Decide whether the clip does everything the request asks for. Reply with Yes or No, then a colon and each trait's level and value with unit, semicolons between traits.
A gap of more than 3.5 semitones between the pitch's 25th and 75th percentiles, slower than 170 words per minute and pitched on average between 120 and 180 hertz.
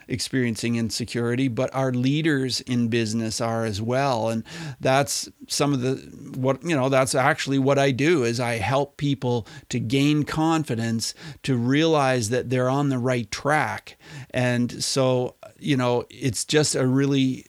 No: narrow, 2.5 semitones; average, 160 wpm; low, 130 Hz